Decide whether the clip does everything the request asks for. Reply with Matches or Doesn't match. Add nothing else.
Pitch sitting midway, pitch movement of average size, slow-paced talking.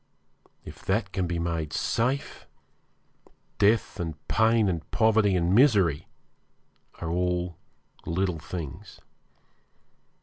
Doesn't match